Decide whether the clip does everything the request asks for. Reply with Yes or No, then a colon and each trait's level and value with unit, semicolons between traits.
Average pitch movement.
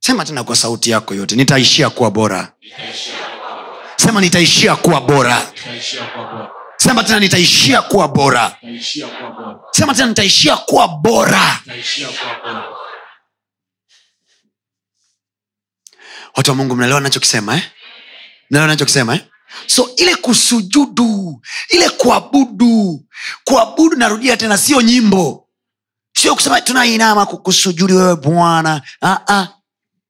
No: wide, 9.0 semitones